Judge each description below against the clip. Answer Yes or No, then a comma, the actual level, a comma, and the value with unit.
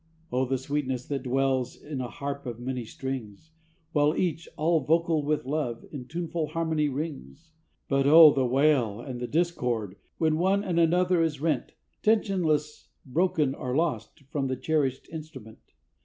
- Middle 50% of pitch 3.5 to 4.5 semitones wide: Yes, average, 3.8 semitones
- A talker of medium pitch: Yes, medium, 145 Hz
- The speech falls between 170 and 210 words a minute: No, average, 155 wpm